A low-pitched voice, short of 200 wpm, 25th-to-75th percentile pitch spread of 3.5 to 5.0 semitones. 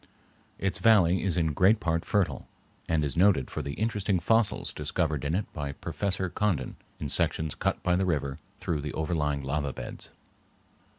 Yes: very low, 85 Hz; average, 170 wpm; average, 4.6 semitones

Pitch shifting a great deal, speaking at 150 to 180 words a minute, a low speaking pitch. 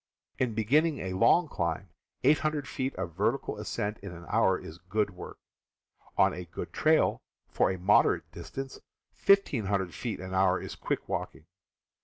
Yes: wide, 6.4 semitones; average, 155 wpm; low, 105 Hz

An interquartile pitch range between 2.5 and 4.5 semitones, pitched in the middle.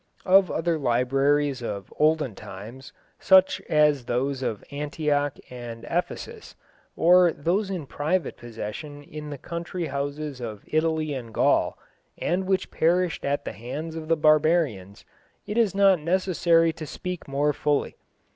Yes: average, 4.1 semitones; medium, 150 Hz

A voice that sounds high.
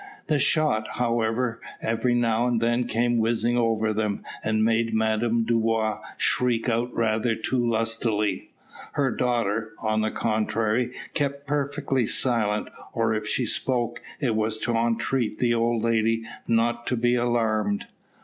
No: low, 115 Hz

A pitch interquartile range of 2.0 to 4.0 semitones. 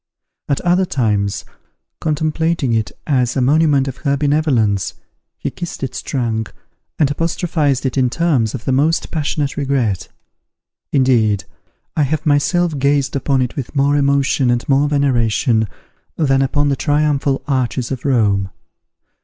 Yes: average, 3.1 semitones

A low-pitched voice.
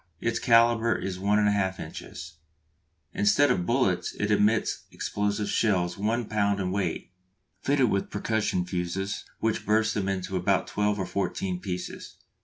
Yes: low, 100 Hz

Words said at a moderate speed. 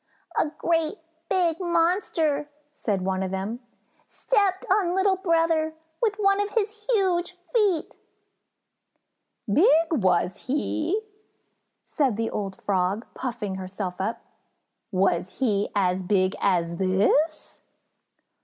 No: slow, 110 wpm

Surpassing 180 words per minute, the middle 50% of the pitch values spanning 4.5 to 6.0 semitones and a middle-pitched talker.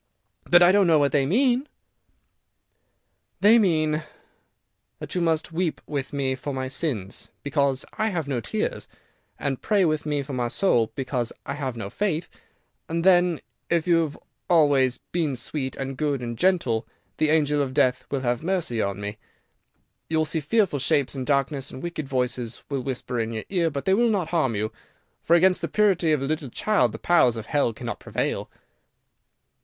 Yes: average, 190 wpm; average, 4.8 semitones; medium, 145 Hz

